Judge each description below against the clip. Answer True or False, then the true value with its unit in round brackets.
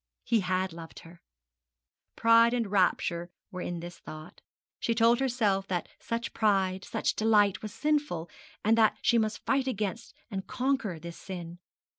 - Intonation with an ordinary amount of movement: True (4.5 semitones)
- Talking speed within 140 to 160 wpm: True (155 wpm)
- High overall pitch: True (205 Hz)